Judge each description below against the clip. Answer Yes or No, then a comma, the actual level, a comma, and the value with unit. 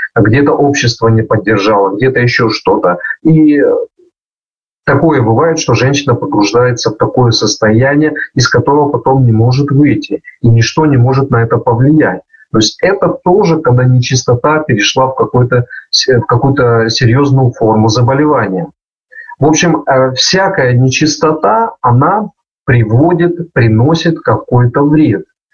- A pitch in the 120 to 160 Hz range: Yes, low, 135 Hz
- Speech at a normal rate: Yes, average, 120 wpm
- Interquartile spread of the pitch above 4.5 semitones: No, average, 4.2 semitones